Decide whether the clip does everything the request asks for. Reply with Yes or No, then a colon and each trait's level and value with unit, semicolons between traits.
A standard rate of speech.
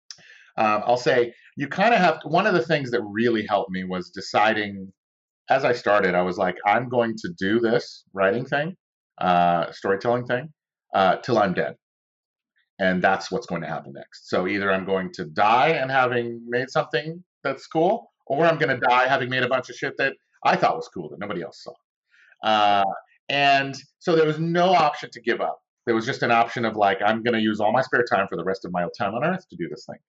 No: fast, 225 wpm